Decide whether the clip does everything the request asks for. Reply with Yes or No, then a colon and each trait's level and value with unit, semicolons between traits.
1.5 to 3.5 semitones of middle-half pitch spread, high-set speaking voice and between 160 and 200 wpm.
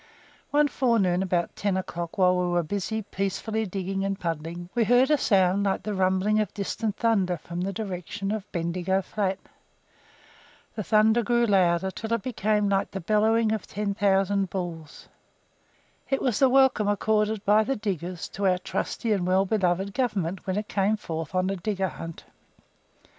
Yes: average, 2.8 semitones; high, 195 Hz; average, 170 wpm